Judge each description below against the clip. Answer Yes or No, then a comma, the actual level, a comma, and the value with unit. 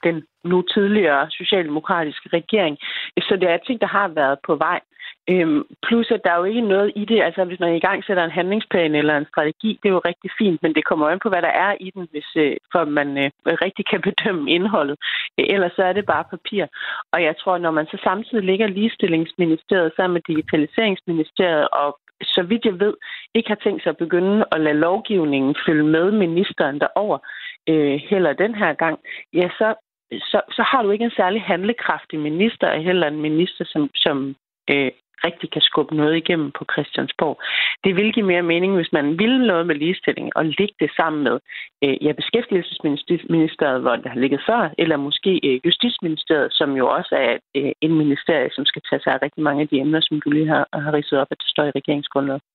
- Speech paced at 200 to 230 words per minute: Yes, average, 210 wpm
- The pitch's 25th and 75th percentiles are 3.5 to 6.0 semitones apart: Yes, average, 4.5 semitones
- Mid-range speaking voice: Yes, medium, 170 Hz